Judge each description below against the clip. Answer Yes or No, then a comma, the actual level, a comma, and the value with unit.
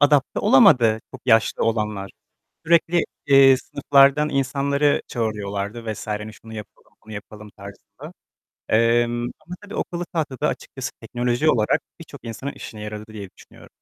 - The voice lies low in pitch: Yes, low, 120 Hz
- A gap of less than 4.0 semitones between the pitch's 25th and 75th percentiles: No, average, 4.7 semitones